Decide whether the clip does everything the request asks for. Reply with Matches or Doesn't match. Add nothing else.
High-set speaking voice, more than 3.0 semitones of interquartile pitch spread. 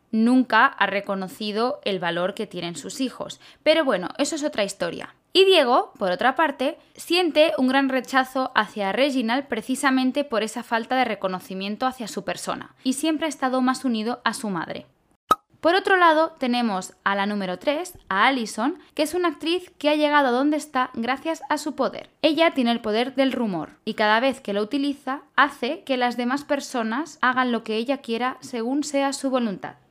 Matches